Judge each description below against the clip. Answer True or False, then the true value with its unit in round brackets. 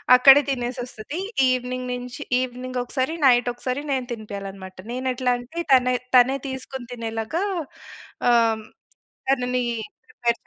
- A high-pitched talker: True (250 Hz)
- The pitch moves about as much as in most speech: False (1.3 semitones)